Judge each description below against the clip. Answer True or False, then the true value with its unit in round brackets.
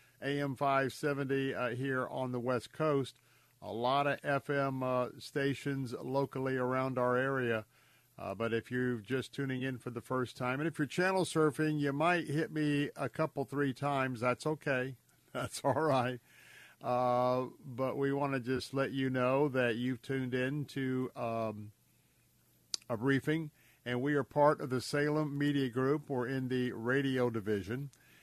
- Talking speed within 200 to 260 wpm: False (165 wpm)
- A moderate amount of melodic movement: False (2.1 semitones)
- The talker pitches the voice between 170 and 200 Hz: False (130 Hz)